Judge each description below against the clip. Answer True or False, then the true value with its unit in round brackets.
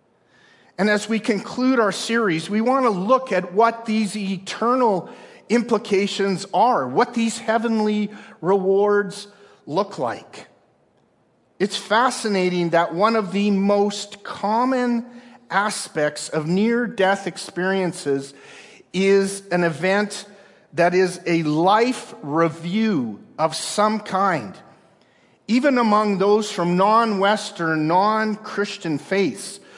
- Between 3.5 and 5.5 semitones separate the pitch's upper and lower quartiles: False (2.8 semitones)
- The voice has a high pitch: True (205 Hz)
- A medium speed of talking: False (110 wpm)